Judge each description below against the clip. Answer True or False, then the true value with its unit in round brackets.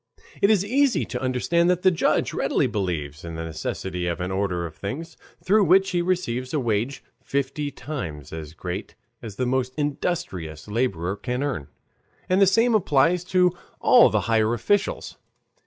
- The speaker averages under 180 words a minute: True (170 wpm)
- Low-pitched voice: True (130 Hz)